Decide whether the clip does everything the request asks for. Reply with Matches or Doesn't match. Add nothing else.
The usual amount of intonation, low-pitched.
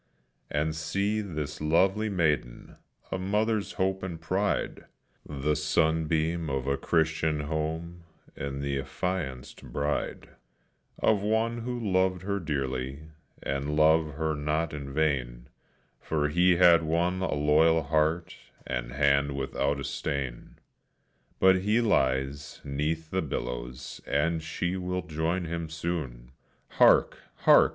Matches